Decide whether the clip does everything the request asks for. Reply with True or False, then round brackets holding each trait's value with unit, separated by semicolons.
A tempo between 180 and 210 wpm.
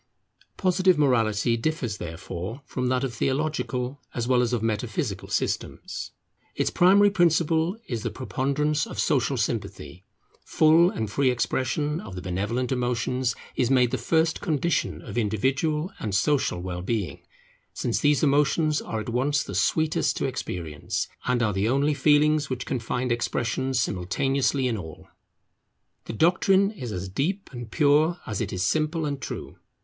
False (155 wpm)